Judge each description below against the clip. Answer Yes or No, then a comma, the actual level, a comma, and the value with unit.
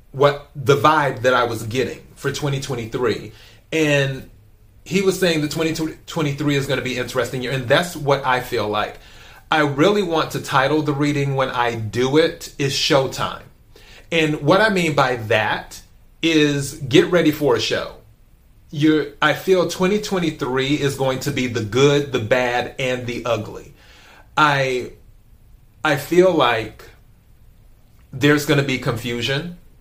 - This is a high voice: No, medium, 140 Hz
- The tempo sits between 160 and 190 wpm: No, average, 150 wpm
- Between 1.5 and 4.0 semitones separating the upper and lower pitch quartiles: Yes, average, 3.6 semitones